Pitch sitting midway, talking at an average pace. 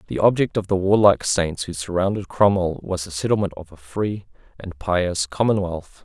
No: very low, 95 Hz; average, 180 wpm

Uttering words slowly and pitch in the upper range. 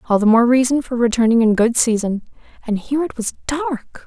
No: fast, 205 wpm; high, 245 Hz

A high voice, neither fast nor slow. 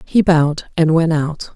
No: medium, 160 Hz; average, 195 wpm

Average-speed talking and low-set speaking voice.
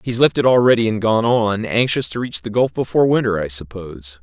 No: fast, 225 wpm; low, 110 Hz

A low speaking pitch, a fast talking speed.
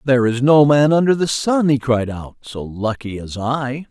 Yes: low, 130 Hz; fast, 215 wpm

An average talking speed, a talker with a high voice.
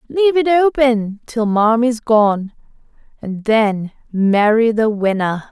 No: slow, 120 wpm; high, 225 Hz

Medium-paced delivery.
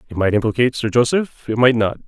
No: fast, 230 wpm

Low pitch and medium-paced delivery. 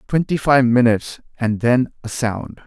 Yes: low, 120 Hz; average, 160 wpm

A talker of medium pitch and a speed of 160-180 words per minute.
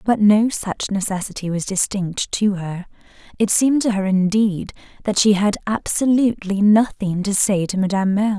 No: high, 200 Hz; average, 165 wpm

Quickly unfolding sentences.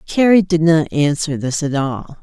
No: average, 190 wpm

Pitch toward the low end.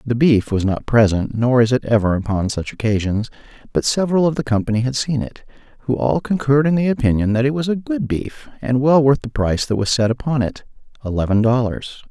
Yes: low, 125 Hz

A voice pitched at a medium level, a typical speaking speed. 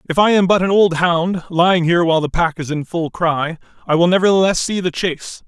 No: medium, 175 Hz; fast, 240 wpm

